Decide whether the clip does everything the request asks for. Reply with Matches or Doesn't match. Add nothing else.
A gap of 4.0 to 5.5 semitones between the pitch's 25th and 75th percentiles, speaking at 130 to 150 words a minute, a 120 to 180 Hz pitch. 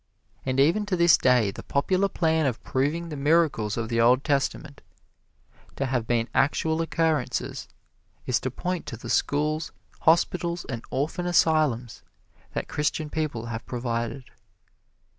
Matches